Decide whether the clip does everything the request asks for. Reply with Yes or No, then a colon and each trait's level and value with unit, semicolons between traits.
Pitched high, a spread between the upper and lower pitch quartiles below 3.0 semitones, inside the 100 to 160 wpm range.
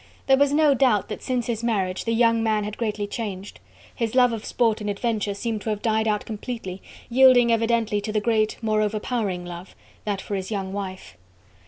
No: high, 220 Hz; narrow, 2.4 semitones; average, 200 wpm